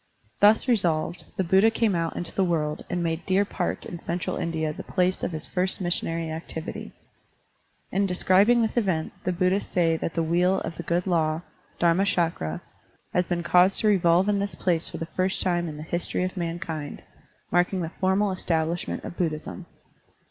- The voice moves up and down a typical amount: No, narrow, 2.3 semitones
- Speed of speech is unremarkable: Yes, average, 185 wpm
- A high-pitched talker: No, medium, 175 Hz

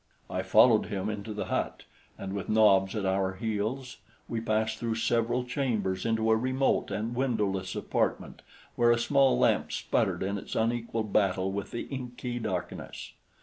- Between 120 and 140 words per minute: No, average, 160 wpm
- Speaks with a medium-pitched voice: No, low, 110 Hz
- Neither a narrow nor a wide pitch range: Yes, average, 3.1 semitones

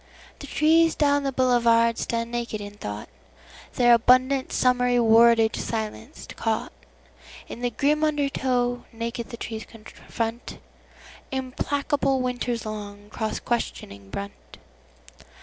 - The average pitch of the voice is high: Yes, high, 235 Hz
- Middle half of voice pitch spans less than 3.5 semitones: Yes, average, 2.8 semitones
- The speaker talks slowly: Yes, slow, 100 wpm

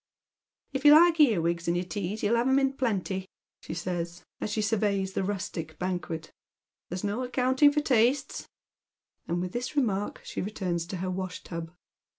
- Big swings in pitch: Yes, wide, 5.8 semitones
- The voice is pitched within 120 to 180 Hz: No, high, 200 Hz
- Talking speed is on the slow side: No, average, 175 wpm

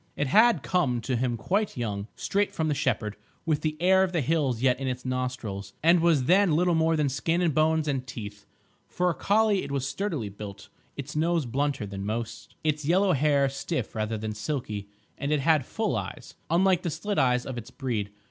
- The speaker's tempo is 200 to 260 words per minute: Yes, fast, 205 wpm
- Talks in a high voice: No, medium, 140 Hz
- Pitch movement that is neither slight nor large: No, wide, 5.9 semitones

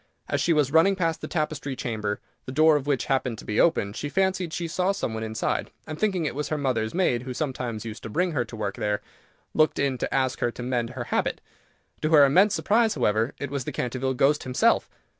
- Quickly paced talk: Yes, fast, 230 wpm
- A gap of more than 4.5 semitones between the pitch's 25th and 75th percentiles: Yes, average, 4.9 semitones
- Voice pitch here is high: No, low, 135 Hz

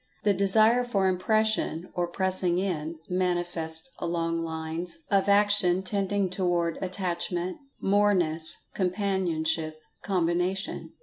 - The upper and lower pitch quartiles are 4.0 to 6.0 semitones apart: No, average, 2.8 semitones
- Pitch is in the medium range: Yes, medium, 180 Hz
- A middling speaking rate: No, slow, 100 wpm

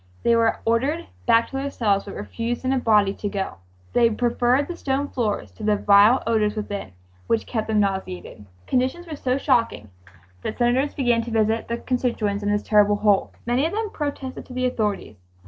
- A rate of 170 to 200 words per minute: Yes, average, 195 wpm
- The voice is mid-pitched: No, high, 230 Hz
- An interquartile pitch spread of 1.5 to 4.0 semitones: Yes, average, 3.7 semitones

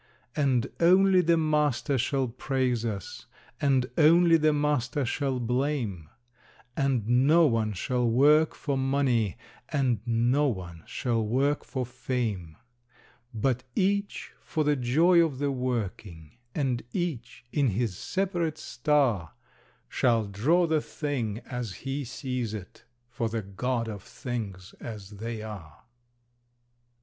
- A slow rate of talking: Yes, slow, 125 wpm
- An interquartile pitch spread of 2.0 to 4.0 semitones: No, average, 4.5 semitones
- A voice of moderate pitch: No, low, 125 Hz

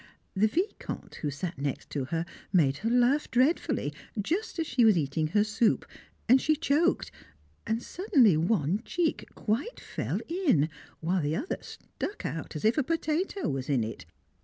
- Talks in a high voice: Yes, high, 220 Hz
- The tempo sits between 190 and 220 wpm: No, average, 165 wpm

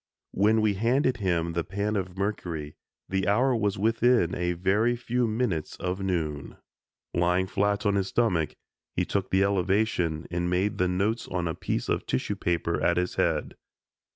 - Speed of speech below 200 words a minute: Yes, average, 170 wpm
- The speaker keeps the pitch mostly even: No, average, 3.5 semitones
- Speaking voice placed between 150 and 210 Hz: No, very low, 95 Hz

